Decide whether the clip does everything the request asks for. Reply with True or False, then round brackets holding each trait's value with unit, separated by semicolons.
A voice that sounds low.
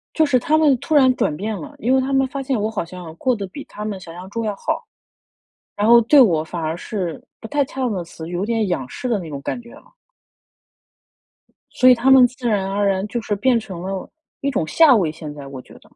False (215 Hz)